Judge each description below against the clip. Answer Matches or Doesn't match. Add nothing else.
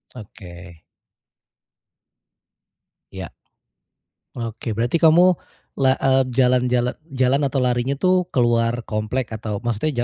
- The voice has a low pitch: Matches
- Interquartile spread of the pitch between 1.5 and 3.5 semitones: Matches